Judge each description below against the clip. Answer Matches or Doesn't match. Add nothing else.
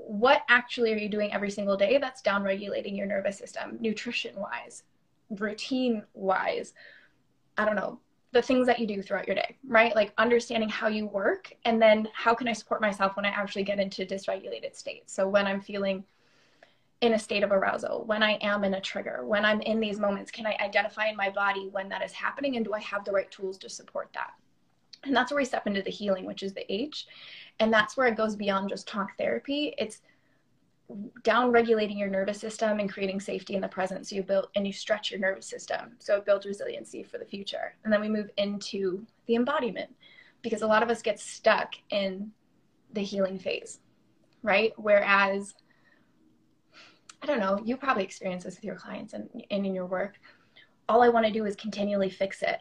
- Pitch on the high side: Matches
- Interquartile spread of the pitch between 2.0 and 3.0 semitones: Matches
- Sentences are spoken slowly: Doesn't match